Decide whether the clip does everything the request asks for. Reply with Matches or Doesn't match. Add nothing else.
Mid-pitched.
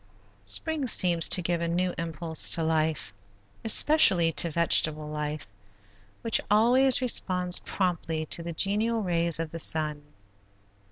Matches